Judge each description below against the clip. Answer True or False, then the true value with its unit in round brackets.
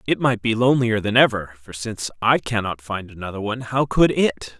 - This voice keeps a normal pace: False (210 wpm)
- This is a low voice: True (110 Hz)